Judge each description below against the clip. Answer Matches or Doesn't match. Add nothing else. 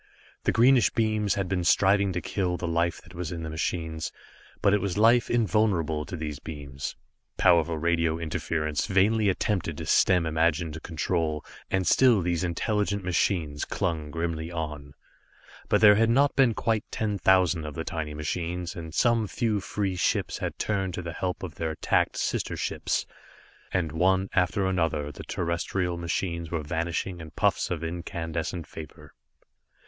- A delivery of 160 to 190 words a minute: Matches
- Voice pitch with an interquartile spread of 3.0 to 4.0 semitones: Matches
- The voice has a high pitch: Doesn't match